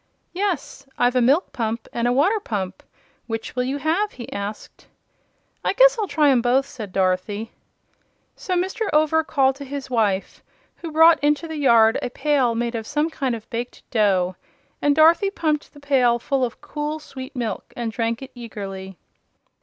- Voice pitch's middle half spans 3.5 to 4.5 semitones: No, average, 4.9 semitones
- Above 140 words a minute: Yes, average, 175 wpm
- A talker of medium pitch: No, very high, 260 Hz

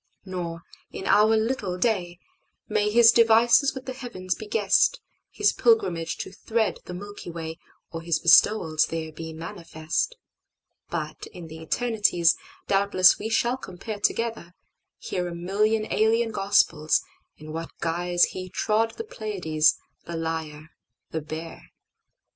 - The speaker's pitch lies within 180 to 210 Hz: Yes, medium, 185 Hz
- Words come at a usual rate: No, slow, 120 wpm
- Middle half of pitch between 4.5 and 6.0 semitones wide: Yes, average, 5.1 semitones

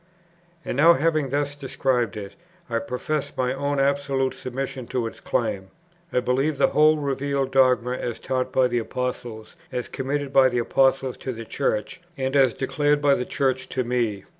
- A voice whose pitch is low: Yes, low, 130 Hz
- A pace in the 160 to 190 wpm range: Yes, average, 175 wpm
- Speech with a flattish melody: Yes, narrow, 2.2 semitones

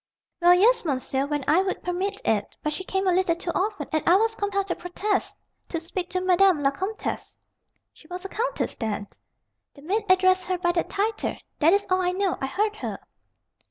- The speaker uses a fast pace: Yes, fast, 210 wpm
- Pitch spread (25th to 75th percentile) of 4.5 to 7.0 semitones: No, average, 2.9 semitones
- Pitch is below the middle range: No, very high, 370 Hz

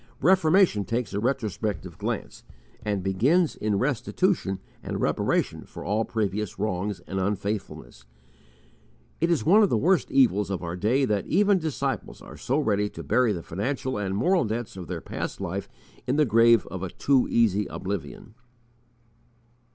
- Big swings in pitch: Yes, wide, 5.7 semitones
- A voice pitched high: No, low, 110 Hz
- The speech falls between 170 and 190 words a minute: No, average, 160 wpm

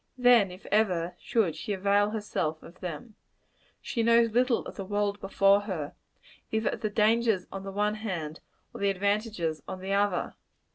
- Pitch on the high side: Yes, high, 205 Hz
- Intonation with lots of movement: No, average, 2.8 semitones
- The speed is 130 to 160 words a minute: No, average, 175 wpm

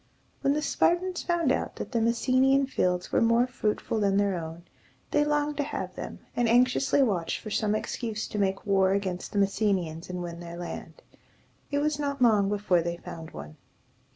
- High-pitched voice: Yes, high, 215 Hz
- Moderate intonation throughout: No, wide, 6.7 semitones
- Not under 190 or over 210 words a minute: Yes, average, 195 wpm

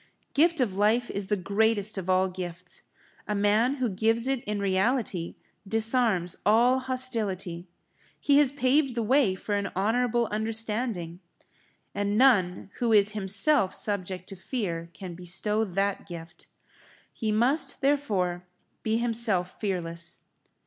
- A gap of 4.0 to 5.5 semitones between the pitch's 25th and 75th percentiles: Yes, average, 4.3 semitones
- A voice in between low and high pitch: No, high, 210 Hz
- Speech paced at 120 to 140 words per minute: Yes, slow, 135 wpm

